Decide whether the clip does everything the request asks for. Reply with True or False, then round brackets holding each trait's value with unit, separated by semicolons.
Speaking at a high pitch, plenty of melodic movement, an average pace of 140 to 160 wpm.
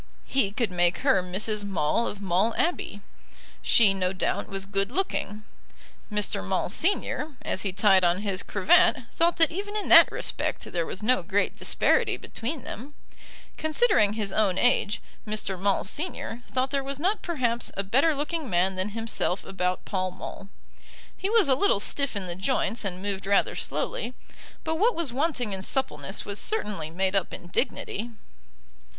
False (210 Hz; 6.4 semitones; 170 wpm)